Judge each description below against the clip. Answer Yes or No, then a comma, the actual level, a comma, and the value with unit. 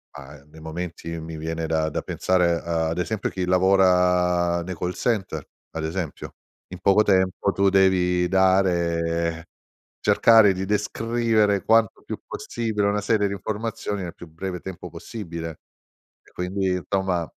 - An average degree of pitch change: Yes, average, 3.0 semitones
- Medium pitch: No, very low, 90 Hz